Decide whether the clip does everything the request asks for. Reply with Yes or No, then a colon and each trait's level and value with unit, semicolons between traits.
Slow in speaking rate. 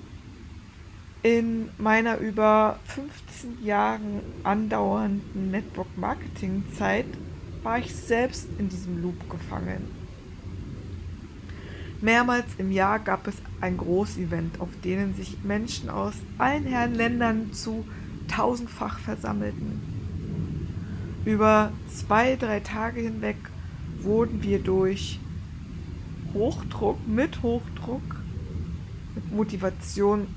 Yes: slow, 90 wpm